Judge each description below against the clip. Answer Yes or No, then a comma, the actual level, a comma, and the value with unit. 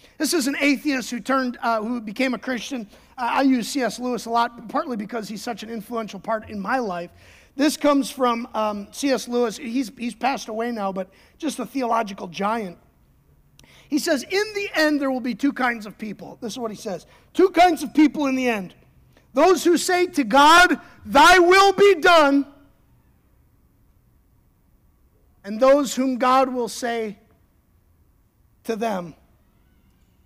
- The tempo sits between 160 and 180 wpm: Yes, average, 170 wpm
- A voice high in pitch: Yes, high, 245 Hz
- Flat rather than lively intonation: No, average, 4.5 semitones